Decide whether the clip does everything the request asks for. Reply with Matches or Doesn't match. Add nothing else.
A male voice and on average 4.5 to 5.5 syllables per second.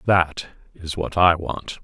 Doesn't match